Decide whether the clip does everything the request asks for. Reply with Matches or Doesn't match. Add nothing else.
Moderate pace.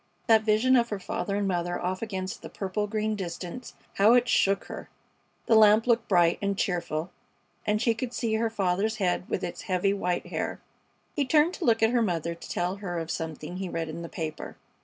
Doesn't match